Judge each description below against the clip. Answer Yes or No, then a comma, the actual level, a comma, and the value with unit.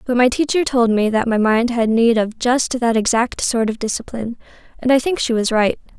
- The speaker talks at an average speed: No, fast, 230 wpm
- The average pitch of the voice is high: Yes, high, 235 Hz